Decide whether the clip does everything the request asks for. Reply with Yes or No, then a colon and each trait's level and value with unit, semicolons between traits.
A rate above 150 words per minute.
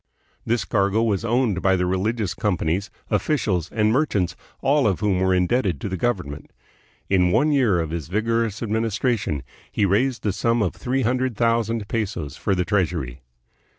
Yes: average, 180 wpm